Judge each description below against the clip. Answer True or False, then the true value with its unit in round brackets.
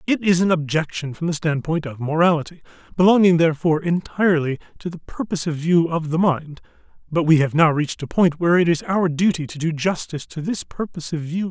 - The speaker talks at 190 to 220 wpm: True (205 wpm)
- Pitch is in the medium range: True (165 Hz)